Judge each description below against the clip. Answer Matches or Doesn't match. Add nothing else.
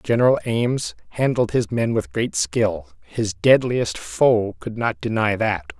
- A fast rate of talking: Doesn't match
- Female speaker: Doesn't match